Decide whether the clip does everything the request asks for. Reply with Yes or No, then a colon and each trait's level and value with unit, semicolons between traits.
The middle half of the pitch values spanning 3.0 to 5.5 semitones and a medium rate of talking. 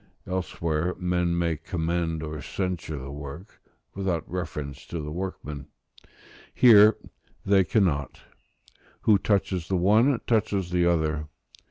No: average, 3.7 semitones; slow, 120 wpm